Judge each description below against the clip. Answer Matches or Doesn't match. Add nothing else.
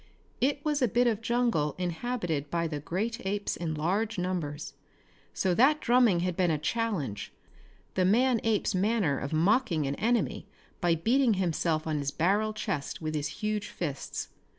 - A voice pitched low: Doesn't match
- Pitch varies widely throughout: Matches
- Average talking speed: Matches